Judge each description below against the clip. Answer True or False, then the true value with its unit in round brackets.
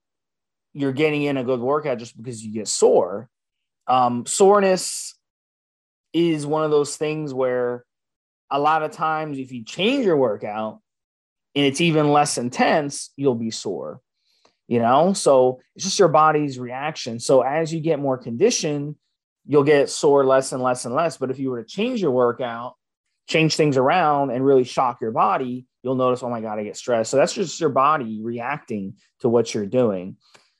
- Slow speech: False (180 wpm)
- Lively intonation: False (4.1 semitones)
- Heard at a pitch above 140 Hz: False (135 Hz)